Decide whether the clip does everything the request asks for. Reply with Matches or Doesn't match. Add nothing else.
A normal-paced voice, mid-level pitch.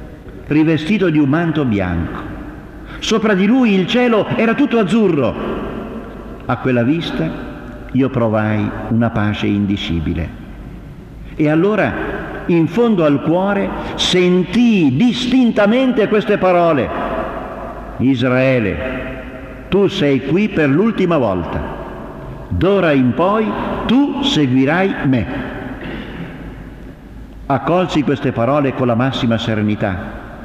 Doesn't match